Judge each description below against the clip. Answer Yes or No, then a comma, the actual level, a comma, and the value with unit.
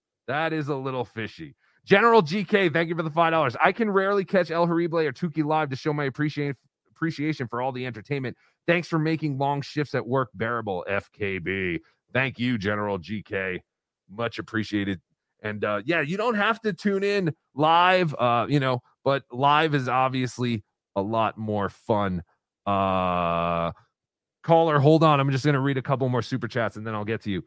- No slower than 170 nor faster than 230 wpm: Yes, average, 190 wpm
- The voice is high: No, medium, 140 Hz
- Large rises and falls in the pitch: Yes, wide, 5.9 semitones